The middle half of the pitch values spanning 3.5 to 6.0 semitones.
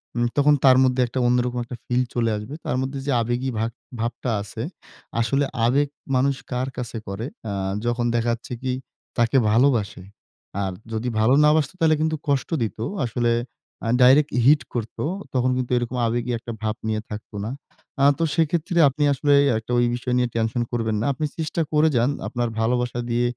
No: average, 2.8 semitones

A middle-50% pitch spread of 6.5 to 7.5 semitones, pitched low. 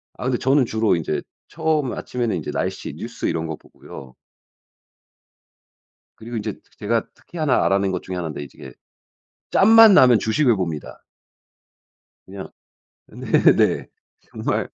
Yes: wide, 6.8 semitones; low, 110 Hz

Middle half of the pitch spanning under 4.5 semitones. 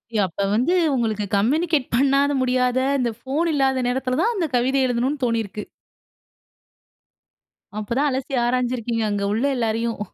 Yes: average, 2.9 semitones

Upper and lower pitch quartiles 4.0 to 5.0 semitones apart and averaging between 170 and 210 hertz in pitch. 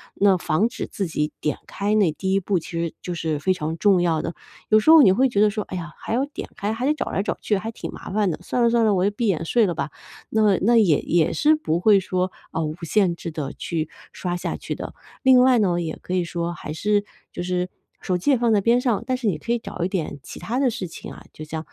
Yes: average, 4.7 semitones; high, 190 Hz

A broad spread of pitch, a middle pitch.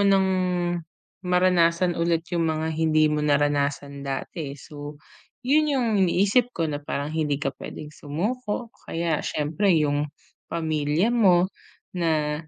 No: average, 3.8 semitones; medium, 160 Hz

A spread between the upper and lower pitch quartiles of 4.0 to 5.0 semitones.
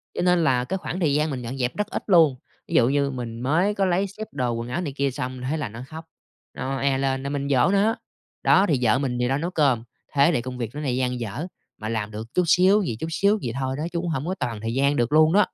No: wide, 5.4 semitones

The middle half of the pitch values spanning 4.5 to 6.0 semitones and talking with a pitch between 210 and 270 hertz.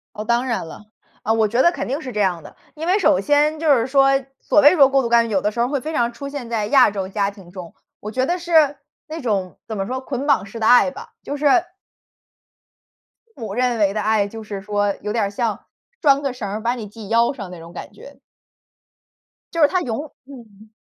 Yes: average, 5.1 semitones; high, 235 Hz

